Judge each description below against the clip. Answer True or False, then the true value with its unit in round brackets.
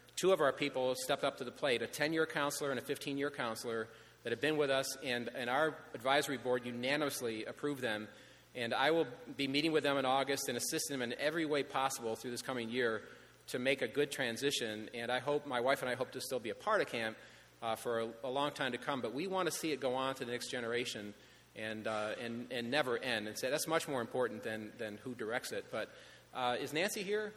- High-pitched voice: False (130 Hz)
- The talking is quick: True (245 wpm)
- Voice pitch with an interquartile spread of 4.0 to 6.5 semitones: False (3.4 semitones)